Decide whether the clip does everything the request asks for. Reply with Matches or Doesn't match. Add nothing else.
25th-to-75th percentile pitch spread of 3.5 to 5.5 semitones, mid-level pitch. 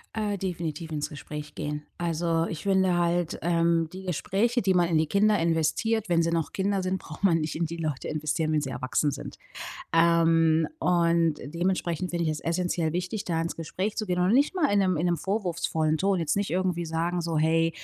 Doesn't match